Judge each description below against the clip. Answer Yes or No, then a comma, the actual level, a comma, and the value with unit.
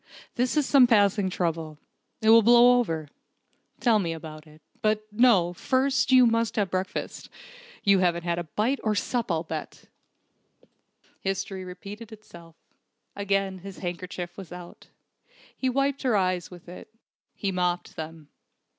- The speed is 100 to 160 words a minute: Yes, average, 145 wpm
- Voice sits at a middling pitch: No, high, 195 Hz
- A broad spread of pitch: No, average, 4.8 semitones